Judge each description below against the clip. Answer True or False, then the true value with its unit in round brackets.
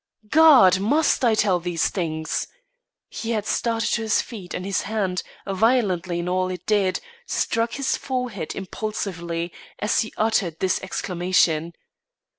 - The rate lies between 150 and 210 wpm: False (140 wpm)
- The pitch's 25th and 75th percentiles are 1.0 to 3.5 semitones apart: False (4.0 semitones)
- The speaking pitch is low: False (195 Hz)